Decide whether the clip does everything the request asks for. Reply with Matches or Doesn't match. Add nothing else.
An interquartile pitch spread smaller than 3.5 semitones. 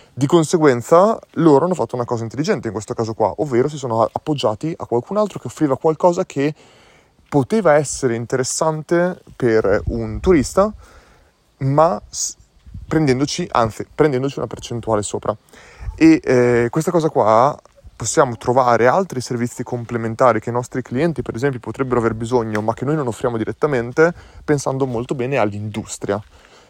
Doesn't match